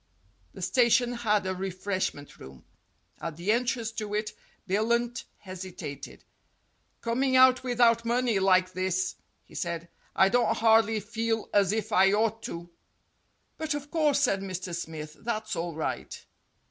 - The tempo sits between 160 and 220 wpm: No, average, 145 wpm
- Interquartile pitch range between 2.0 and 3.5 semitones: No, average, 4.2 semitones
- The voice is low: No, high, 210 Hz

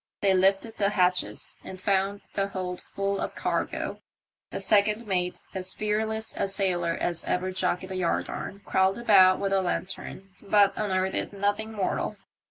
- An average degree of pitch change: No, narrow, 1.5 semitones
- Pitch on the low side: No, high, 195 Hz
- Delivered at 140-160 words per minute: Yes, average, 155 wpm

